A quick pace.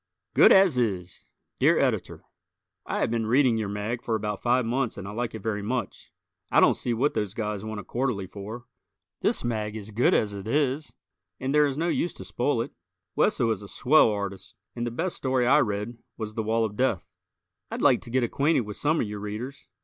Yes: fast, 220 wpm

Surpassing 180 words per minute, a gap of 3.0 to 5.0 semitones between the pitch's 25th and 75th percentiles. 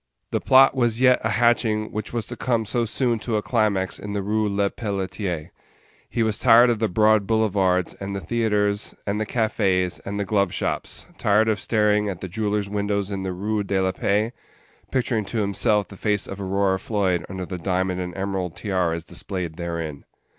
No: average, 190 wpm; narrow, 2.5 semitones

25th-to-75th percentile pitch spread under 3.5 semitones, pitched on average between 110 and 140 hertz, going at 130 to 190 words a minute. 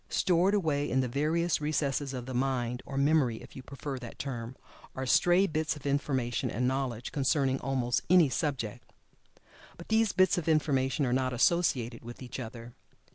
No: average, 3.8 semitones; low, 135 Hz; average, 175 wpm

